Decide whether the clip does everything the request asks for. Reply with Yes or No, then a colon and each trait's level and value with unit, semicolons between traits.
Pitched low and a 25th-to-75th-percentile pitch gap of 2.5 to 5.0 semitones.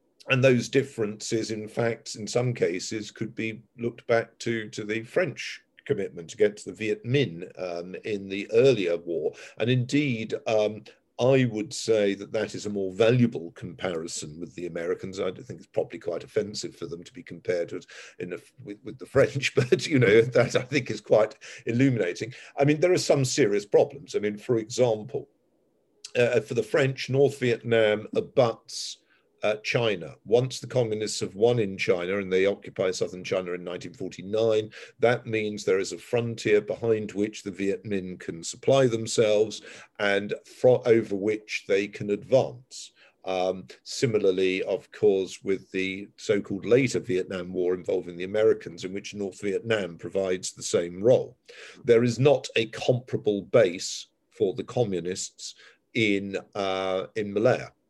Yes: low, 110 Hz; average, 3.7 semitones